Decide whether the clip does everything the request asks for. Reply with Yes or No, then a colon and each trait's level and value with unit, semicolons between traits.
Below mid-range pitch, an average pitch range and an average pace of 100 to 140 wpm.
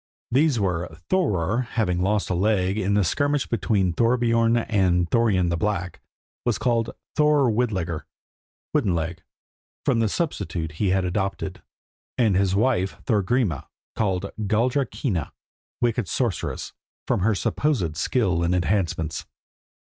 Yes: low, 100 Hz; average, 4.7 semitones; slow, 135 wpm